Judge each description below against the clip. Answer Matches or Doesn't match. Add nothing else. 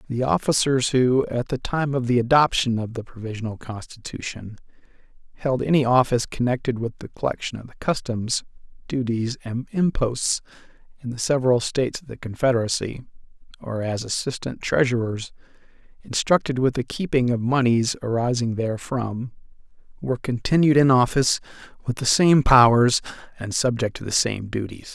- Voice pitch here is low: Matches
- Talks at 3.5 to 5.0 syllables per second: Doesn't match